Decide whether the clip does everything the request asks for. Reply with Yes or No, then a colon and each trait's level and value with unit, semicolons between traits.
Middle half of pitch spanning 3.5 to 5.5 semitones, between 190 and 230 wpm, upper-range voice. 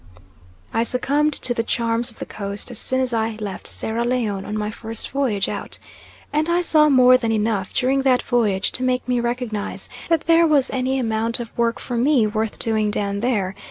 No: average, 3.0 semitones; average, 200 wpm; high, 235 Hz